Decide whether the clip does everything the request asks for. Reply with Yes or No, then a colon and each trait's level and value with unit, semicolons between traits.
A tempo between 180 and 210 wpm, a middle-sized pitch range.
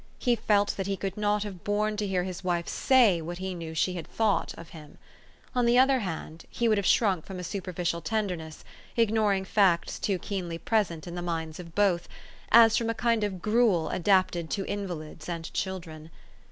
Yes: average, 195 wpm; average, 3.7 semitones